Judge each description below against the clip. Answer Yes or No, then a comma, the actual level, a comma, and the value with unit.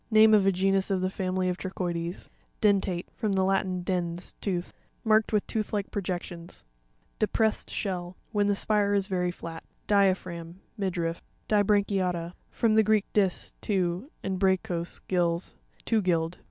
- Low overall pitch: No, high, 190 Hz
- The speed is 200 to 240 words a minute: No, average, 145 wpm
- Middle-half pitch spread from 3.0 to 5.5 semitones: No, narrow, 2.5 semitones